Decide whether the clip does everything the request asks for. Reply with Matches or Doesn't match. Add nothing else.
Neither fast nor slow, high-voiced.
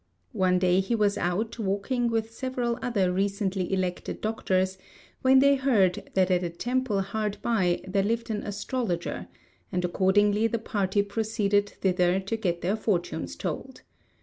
Matches